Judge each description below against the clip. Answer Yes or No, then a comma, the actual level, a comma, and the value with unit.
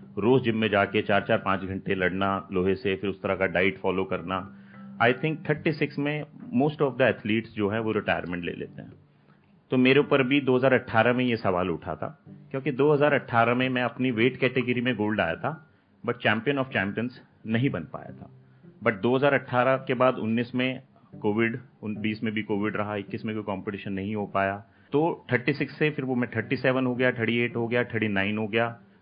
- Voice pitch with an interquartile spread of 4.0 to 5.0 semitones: Yes, average, 4.6 semitones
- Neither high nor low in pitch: No, low, 115 Hz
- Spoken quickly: Yes, fast, 220 wpm